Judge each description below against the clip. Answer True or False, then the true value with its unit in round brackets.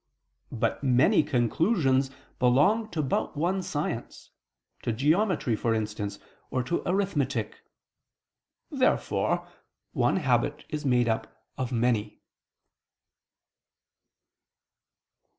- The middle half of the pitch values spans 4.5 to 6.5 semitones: True (4.9 semitones)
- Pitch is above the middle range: False (130 Hz)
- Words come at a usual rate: False (90 wpm)